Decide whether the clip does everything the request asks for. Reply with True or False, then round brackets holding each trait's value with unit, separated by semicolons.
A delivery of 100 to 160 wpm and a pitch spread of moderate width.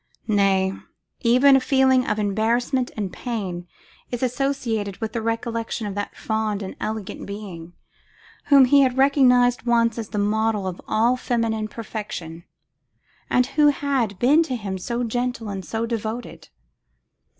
True (145 wpm; 3.3 semitones)